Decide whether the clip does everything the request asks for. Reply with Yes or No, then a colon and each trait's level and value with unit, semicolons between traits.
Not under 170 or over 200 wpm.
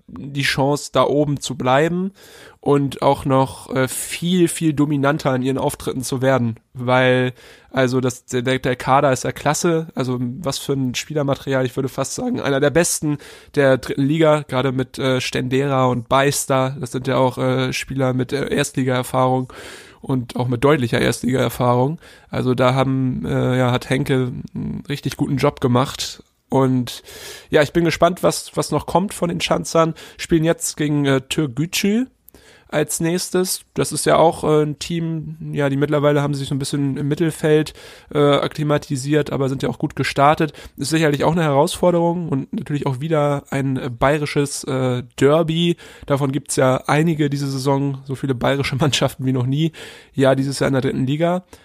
Yes: average, 180 wpm